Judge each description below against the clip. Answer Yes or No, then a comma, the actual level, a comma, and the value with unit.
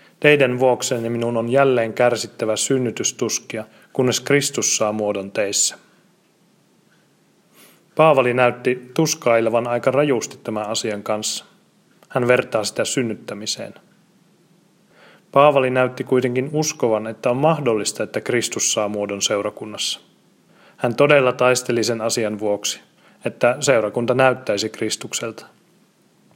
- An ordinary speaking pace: Yes, average, 105 wpm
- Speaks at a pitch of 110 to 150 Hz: Yes, low, 125 Hz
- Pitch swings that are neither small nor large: Yes, average, 3.8 semitones